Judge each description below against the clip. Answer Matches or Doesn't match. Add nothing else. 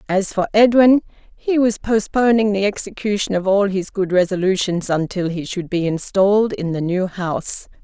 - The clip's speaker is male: Doesn't match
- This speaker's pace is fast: Doesn't match